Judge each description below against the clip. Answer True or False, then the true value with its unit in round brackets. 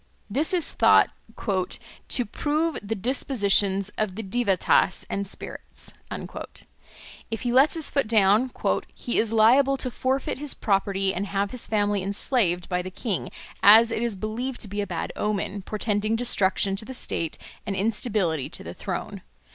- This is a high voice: True (215 Hz)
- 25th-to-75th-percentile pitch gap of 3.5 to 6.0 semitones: True (3.9 semitones)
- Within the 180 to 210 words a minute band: False (160 wpm)